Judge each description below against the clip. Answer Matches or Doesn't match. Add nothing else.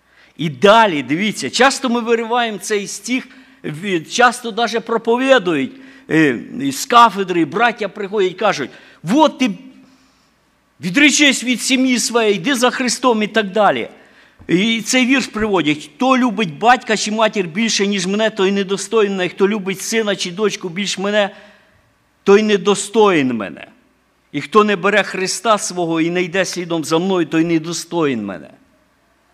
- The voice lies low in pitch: Doesn't match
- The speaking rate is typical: Matches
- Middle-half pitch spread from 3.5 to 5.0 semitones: Matches